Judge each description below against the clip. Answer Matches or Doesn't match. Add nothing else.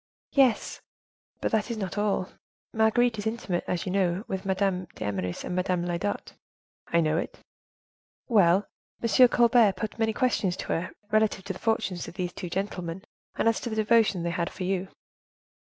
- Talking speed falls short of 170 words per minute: Doesn't match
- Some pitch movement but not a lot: Matches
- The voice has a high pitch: Matches